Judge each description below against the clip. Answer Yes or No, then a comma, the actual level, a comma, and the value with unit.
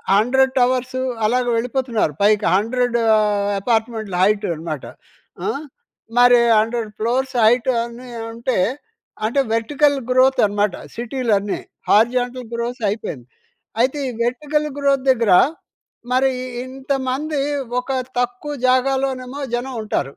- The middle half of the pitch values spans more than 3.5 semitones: No, average, 2.9 semitones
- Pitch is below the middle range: No, high, 245 Hz